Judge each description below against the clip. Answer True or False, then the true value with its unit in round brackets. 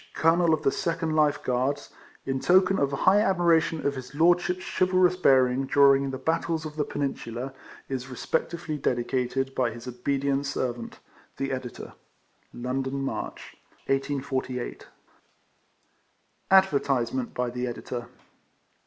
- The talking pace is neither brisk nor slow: False (125 wpm)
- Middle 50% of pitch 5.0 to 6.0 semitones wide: False (4.0 semitones)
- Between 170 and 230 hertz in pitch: False (135 Hz)